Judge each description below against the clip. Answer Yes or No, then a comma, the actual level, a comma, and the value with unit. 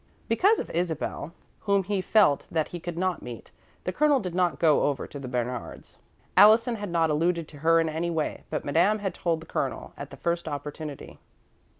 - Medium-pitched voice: Yes, medium, 170 Hz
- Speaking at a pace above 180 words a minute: Yes, average, 195 wpm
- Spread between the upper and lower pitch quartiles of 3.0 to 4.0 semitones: Yes, average, 3.6 semitones